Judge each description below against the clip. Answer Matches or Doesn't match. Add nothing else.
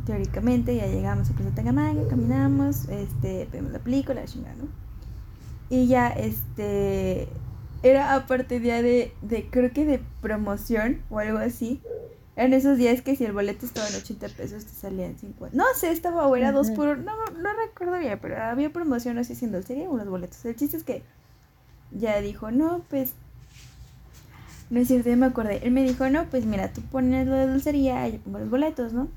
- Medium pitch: Doesn't match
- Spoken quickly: Matches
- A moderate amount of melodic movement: Doesn't match